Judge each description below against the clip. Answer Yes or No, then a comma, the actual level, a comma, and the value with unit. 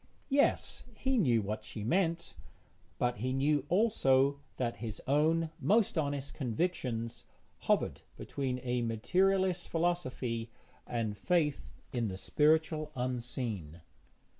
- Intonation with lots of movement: Yes, wide, 6.0 semitones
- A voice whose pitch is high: No, low, 135 Hz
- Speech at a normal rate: No, slow, 115 wpm